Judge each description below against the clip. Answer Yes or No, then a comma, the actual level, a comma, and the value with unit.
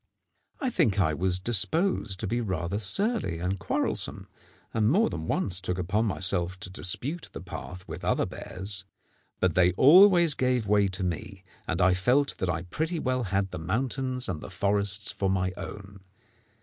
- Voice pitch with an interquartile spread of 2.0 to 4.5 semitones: No, wide, 5.5 semitones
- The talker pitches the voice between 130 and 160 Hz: No, low, 100 Hz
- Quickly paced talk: No, average, 175 wpm